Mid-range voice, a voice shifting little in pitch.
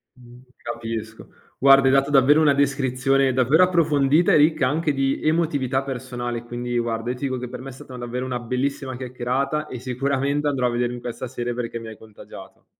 No: low, 130 Hz; narrow, 2.3 semitones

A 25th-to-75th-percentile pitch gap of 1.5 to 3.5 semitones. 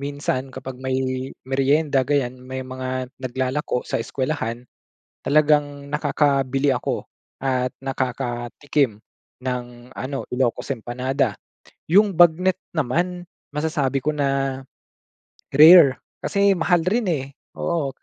Yes: average, 2.8 semitones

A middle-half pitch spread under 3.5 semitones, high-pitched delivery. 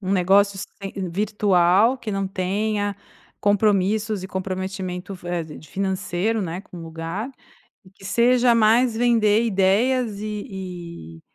Yes: average, 2.7 semitones; high, 195 Hz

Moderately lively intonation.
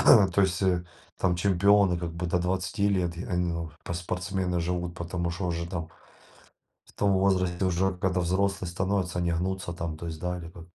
No: narrow, 1.7 semitones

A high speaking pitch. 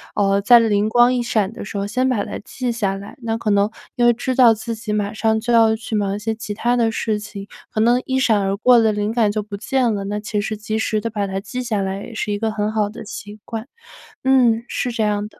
Yes: high, 220 Hz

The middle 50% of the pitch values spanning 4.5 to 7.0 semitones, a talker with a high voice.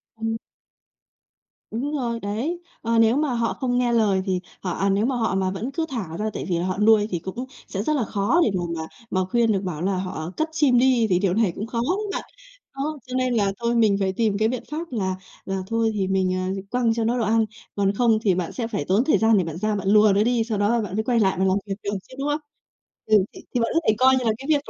No: average, 3.9 semitones; high, 220 Hz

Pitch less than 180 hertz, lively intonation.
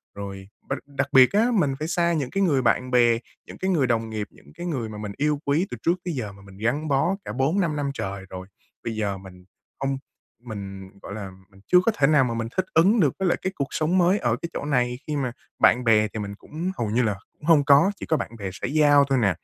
Yes: low, 135 Hz; wide, 6.5 semitones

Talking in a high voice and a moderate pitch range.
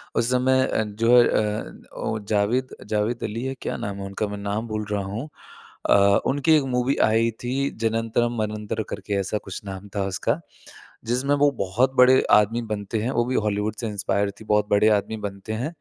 No: low, 110 Hz; average, 3.1 semitones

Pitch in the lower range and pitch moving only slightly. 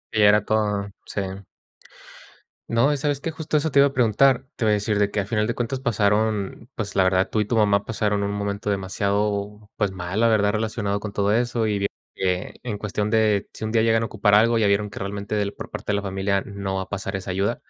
Yes: low, 105 Hz; narrow, 2.0 semitones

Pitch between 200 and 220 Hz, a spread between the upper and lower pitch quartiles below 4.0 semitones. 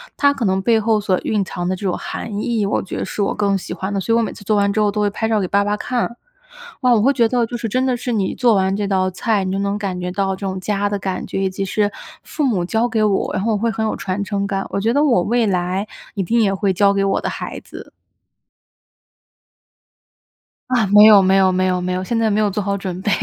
Yes: high, 205 Hz; narrow, 2.5 semitones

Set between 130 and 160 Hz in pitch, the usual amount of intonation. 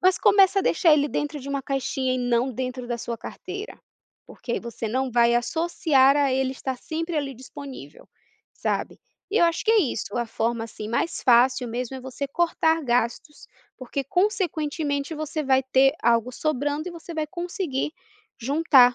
No: very high, 270 Hz; average, 4.4 semitones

